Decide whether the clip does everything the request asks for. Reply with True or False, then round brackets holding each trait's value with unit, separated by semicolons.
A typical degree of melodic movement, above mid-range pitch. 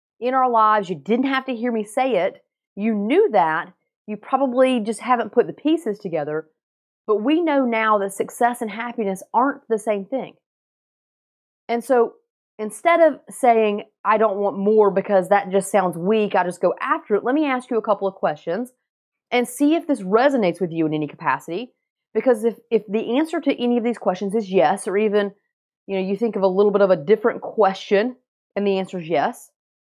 True (4.2 semitones; 220 Hz)